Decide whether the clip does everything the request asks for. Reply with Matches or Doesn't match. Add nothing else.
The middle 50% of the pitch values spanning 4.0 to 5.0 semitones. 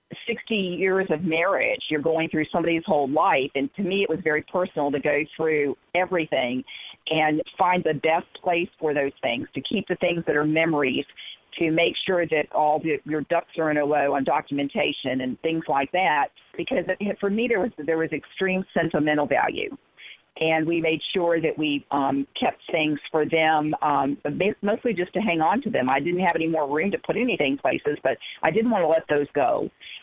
Doesn't match